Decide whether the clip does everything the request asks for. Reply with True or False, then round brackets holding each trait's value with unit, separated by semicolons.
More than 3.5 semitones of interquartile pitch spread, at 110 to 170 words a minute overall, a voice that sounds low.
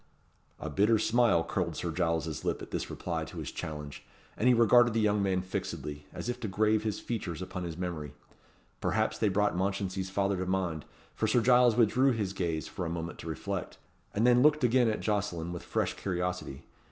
False (4.4 semitones; 200 wpm; 95 Hz)